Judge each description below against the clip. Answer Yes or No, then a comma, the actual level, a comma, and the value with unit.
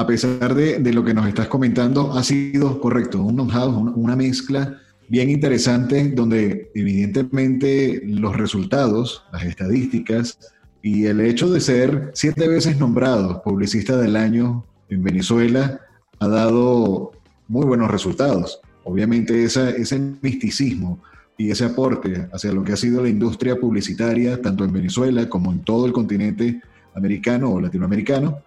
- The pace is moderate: Yes, average, 145 wpm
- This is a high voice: No, low, 120 Hz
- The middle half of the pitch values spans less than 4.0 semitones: Yes, average, 3.6 semitones